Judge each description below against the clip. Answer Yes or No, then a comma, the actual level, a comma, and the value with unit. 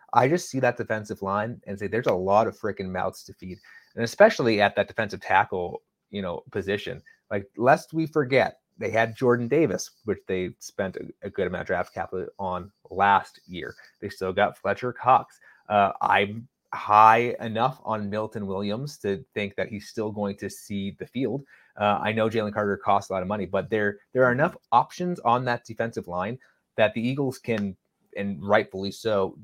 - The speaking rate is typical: Yes, average, 195 wpm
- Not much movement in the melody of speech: No, average, 3.4 semitones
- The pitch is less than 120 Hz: Yes, low, 110 Hz